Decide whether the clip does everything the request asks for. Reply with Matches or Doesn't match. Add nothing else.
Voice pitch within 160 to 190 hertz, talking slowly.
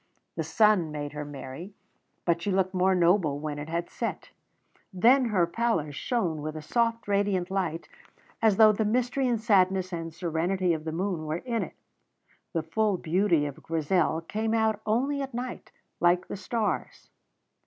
Doesn't match